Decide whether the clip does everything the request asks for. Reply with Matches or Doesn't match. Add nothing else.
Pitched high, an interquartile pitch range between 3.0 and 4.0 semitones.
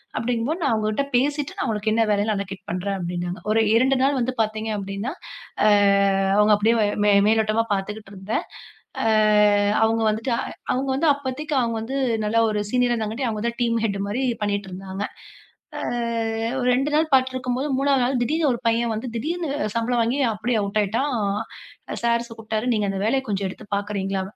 Matches